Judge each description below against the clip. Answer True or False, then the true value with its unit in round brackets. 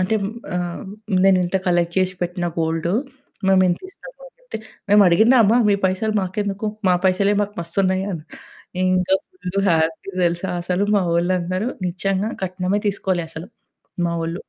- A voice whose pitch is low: False (185 Hz)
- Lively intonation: False (2.4 semitones)